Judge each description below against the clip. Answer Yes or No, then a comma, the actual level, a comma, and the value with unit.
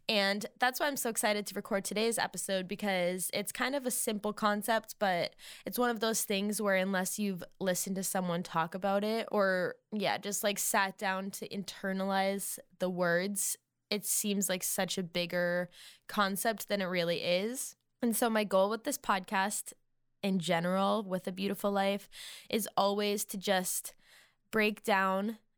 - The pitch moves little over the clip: Yes, narrow, 2.3 semitones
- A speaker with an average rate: Yes, average, 170 wpm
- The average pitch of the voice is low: No, high, 200 Hz